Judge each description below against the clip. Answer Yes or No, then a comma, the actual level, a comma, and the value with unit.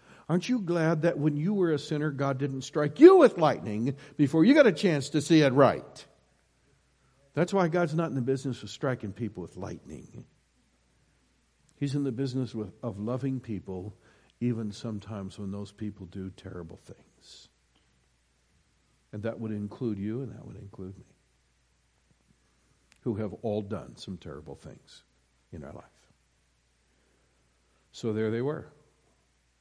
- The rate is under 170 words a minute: Yes, average, 150 wpm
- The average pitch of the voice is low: Yes, low, 110 Hz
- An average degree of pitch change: No, wide, 8.8 semitones